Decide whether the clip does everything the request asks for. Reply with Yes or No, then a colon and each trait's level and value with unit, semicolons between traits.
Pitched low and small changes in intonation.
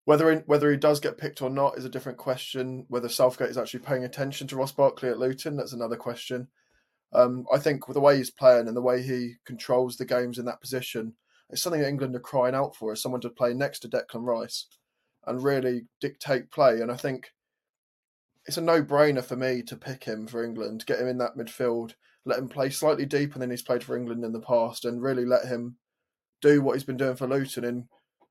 Yes: low, 125 Hz; narrow, 2.1 semitones